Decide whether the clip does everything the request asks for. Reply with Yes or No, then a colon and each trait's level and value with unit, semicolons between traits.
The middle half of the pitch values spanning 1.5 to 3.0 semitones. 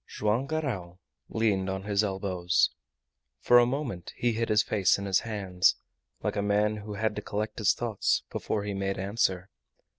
Yes: narrow, 2.5 semitones